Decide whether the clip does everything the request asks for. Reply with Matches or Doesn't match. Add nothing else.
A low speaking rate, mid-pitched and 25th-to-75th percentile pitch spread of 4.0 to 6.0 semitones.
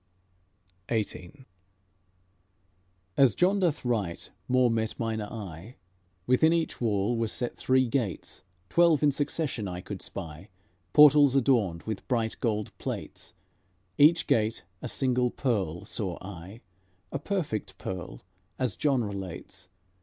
Doesn't match